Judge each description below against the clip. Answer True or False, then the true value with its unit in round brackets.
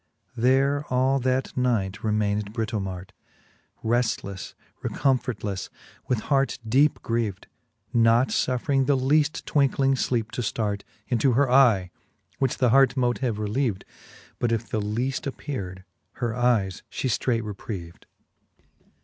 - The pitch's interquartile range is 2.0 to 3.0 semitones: False (3.9 semitones)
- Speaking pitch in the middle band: False (120 Hz)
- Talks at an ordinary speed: False (125 wpm)